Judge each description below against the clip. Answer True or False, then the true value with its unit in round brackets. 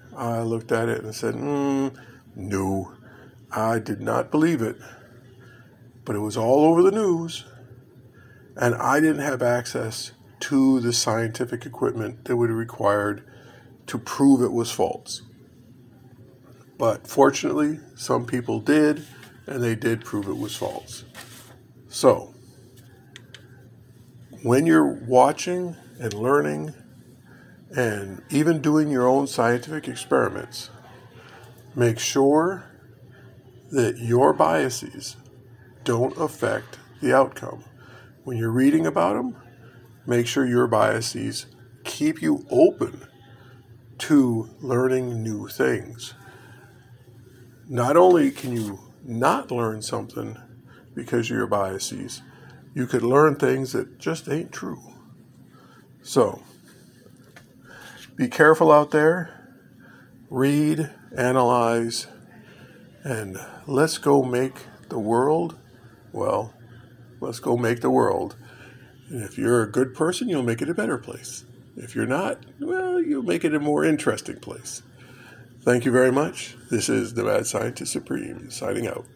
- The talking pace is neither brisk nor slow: False (120 wpm)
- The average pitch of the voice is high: False (125 Hz)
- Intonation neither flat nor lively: False (2.0 semitones)